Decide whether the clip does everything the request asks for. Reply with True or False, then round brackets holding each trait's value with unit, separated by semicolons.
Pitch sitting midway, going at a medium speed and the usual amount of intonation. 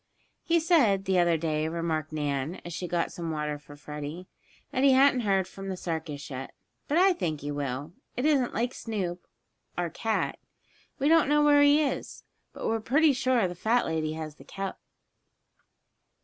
False (180 Hz; 180 wpm; 8.8 semitones)